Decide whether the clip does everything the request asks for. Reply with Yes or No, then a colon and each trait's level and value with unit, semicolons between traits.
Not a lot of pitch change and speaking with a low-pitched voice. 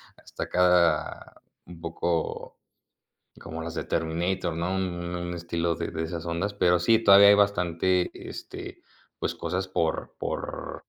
Yes: narrow, 1.8 semitones; very low, 85 Hz